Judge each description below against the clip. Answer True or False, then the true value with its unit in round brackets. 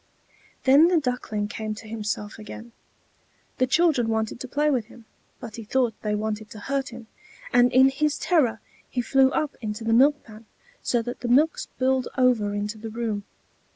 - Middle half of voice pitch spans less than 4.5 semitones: True (3.5 semitones)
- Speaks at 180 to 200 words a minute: True (185 wpm)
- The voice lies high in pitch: True (240 Hz)